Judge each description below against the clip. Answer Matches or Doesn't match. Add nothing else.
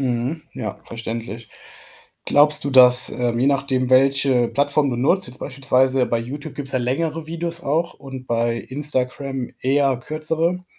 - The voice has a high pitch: Doesn't match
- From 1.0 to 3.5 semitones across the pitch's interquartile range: Matches